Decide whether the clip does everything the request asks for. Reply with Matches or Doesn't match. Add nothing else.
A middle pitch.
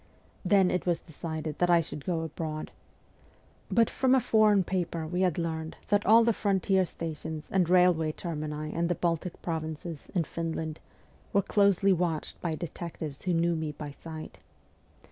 Matches